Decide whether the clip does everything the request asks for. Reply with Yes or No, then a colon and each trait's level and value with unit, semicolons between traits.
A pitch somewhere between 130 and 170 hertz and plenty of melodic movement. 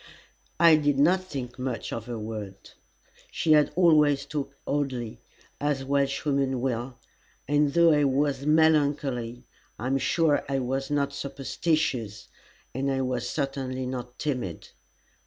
No: low, 135 Hz; narrow, 2.6 semitones